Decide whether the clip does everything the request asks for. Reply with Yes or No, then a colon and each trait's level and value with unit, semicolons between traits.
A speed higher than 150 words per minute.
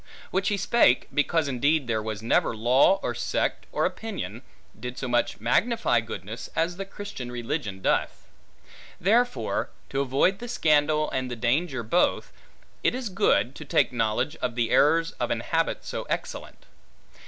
Yes: average, 160 wpm